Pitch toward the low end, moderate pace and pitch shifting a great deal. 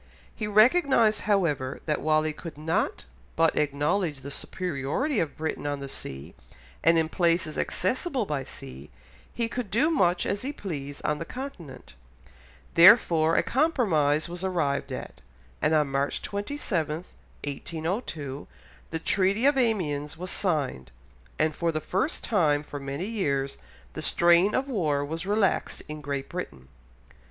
No: medium, 165 Hz; average, 145 wpm; wide, 5.8 semitones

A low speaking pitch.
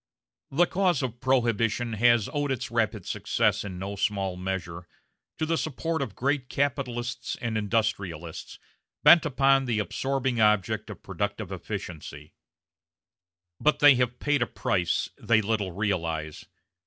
Yes: low, 115 Hz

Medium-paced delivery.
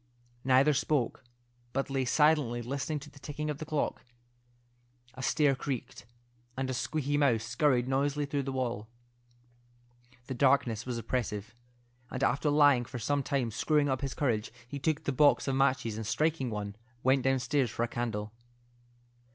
Yes: average, 160 wpm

